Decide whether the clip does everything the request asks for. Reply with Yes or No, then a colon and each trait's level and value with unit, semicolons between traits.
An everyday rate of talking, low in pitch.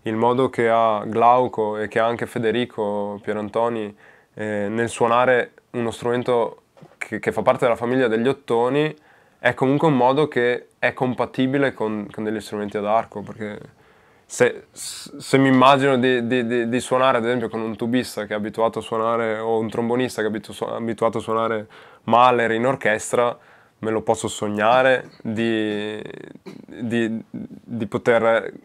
Yes: average, 160 wpm; low, 115 Hz